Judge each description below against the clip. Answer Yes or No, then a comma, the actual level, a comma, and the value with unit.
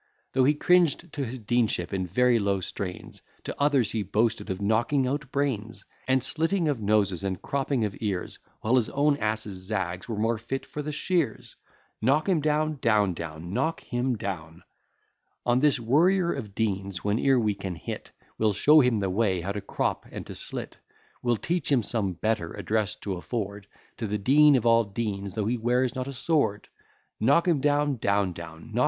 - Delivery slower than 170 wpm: No, average, 175 wpm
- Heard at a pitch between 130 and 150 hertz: No, low, 115 Hz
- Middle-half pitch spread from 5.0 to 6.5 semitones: Yes, wide, 5.5 semitones